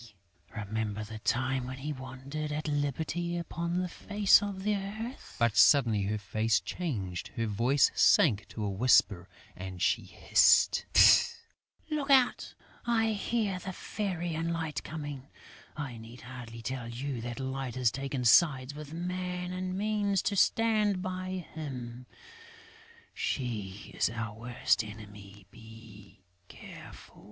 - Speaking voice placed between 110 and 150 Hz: Yes, low, 135 Hz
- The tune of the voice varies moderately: No, wide, 8.1 semitones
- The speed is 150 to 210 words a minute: No, slow, 135 wpm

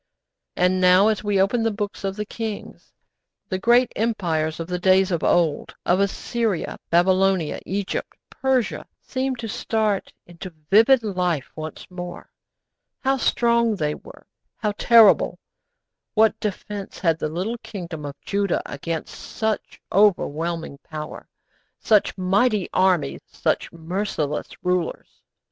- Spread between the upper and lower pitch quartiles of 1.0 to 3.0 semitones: No, average, 4.1 semitones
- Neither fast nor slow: No, slow, 130 wpm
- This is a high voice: Yes, high, 195 Hz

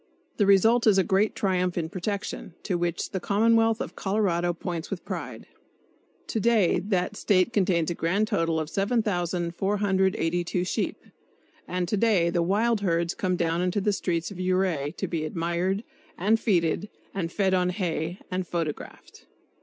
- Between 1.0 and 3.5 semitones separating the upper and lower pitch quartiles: Yes, average, 3.0 semitones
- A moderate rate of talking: Yes, average, 160 wpm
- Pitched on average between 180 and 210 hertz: Yes, medium, 185 Hz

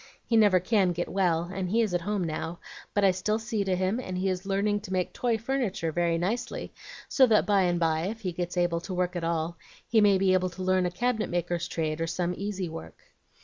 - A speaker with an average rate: No, fast, 240 wpm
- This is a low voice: No, medium, 185 Hz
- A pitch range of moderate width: Yes, average, 3.0 semitones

